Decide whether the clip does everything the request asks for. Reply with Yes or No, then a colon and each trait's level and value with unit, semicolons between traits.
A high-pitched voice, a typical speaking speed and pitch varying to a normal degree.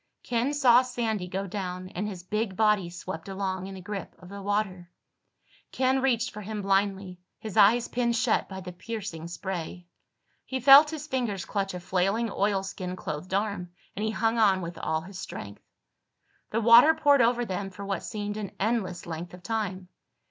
Yes: high, 200 Hz; average, 180 wpm; average, 3.7 semitones